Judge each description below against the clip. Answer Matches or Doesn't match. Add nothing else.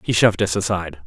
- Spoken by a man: Matches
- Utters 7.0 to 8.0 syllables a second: Matches